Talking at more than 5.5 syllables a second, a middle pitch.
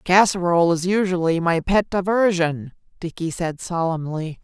No: 4.7 syllables/s; medium, 175 Hz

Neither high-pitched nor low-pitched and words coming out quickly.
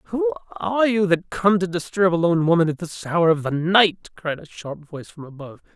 Yes: medium, 170 Hz; fast, 230 wpm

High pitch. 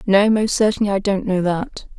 Yes: high, 200 Hz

